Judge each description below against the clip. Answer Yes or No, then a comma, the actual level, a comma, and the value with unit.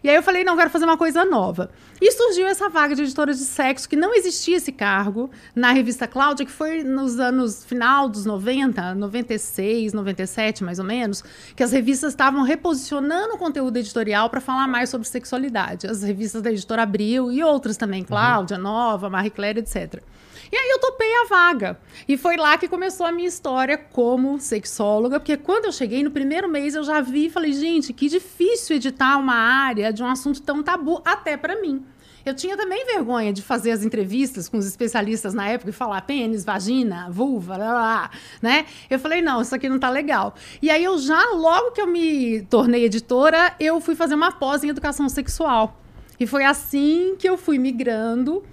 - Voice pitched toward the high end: Yes, very high, 270 Hz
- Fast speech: Yes, fast, 200 wpm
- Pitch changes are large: Yes, wide, 5.7 semitones